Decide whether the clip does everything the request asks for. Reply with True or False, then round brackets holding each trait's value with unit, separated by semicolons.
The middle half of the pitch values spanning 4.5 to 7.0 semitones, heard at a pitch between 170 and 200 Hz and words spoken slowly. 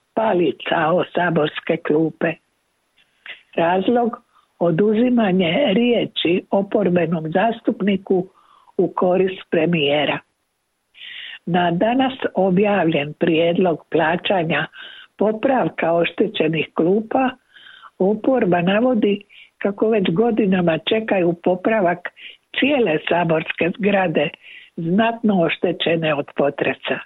True (5.1 semitones; 190 Hz; 75 wpm)